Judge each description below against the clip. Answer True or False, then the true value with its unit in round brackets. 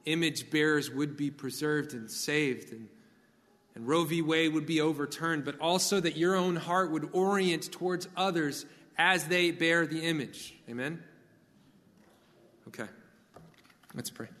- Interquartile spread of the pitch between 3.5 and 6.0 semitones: False (2.8 semitones)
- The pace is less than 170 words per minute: True (140 wpm)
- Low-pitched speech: False (160 Hz)